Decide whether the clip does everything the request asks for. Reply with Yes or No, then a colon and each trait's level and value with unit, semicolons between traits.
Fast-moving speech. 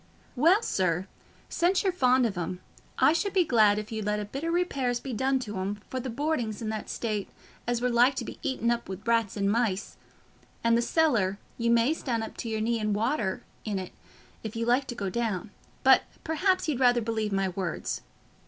Yes: fast, 210 wpm